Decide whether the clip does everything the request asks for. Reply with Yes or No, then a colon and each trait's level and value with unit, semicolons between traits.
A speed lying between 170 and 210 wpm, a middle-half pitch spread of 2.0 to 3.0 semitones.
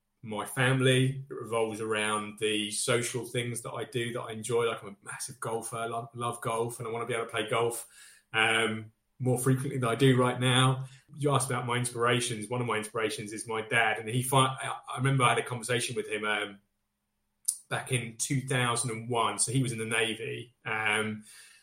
Yes: fast, 205 wpm; narrow, 2.4 semitones